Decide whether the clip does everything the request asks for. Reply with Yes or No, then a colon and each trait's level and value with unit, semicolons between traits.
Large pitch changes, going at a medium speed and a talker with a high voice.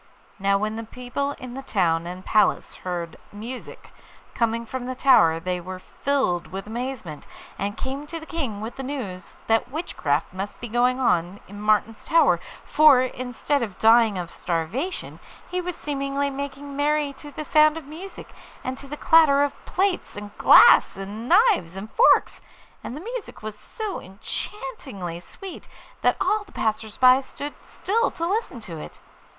Yes: wide, 6.3 semitones; average, 170 wpm; very high, 250 Hz